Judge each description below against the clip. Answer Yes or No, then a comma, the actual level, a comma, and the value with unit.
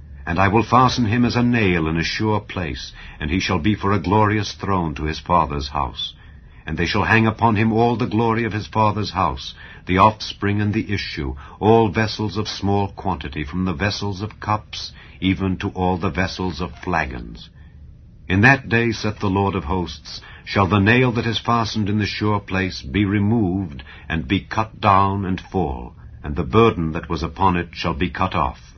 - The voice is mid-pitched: No, very low, 95 Hz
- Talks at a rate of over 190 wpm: Yes, average, 200 wpm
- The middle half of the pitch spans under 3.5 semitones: No, average, 4.4 semitones